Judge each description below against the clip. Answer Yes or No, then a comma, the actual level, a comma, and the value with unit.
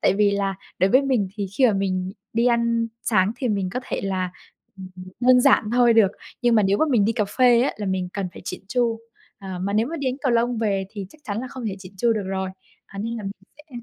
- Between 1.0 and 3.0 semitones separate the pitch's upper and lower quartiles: No, average, 3.9 semitones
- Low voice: No, high, 215 Hz